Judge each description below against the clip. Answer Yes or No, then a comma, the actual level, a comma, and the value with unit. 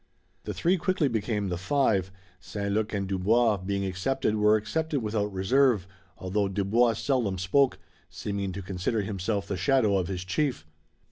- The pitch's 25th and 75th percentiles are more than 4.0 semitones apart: No, average, 3.7 semitones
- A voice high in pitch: No, low, 105 Hz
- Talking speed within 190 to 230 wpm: No, average, 155 wpm